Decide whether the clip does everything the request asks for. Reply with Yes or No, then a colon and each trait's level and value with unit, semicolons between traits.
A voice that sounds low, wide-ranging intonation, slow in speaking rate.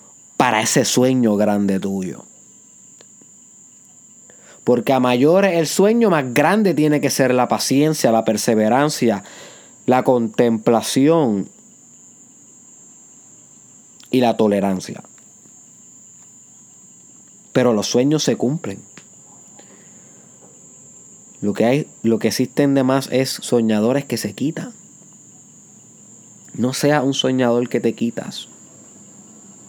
No: low, 125 Hz; average, 4.1 semitones; slow, 100 wpm